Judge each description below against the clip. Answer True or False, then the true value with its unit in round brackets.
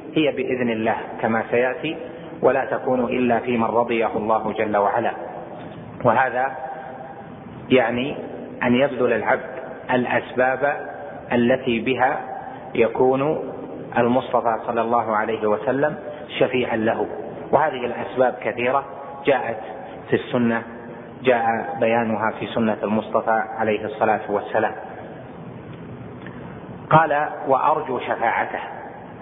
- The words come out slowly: False (95 wpm)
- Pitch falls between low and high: False (120 Hz)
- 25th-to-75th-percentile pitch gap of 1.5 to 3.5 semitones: True (2.7 semitones)